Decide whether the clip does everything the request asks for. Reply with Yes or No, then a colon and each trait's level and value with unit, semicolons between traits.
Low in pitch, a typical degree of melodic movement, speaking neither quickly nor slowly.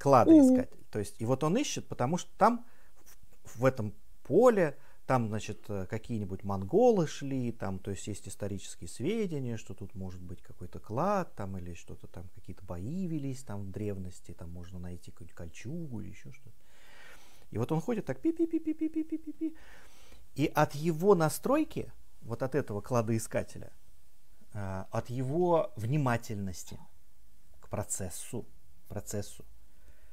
No: low, 110 Hz; wide, 8.5 semitones; average, 135 wpm